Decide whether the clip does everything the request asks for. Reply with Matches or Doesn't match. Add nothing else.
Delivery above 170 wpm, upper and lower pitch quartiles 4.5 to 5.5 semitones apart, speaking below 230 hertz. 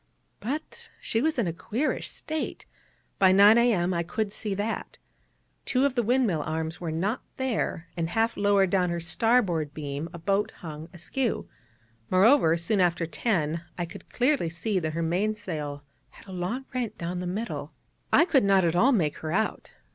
Matches